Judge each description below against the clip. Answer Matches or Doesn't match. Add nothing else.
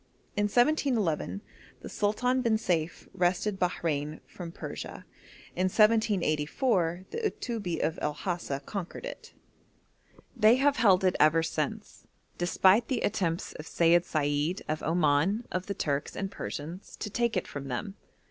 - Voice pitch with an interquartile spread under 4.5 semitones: Doesn't match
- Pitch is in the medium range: Matches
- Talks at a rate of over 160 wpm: Doesn't match